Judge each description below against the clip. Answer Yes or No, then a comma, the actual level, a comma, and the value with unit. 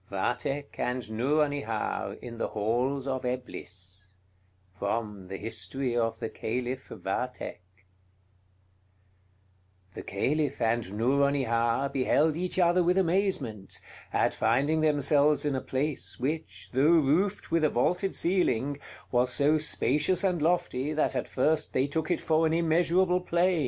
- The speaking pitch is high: No, medium, 140 Hz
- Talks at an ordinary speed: No, slow, 130 wpm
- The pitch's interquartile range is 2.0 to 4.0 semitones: No, average, 5.2 semitones